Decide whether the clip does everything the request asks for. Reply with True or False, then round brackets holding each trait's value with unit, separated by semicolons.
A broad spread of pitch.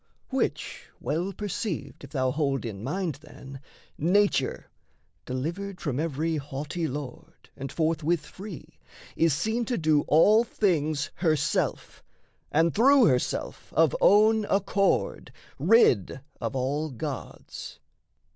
True (5.9 semitones)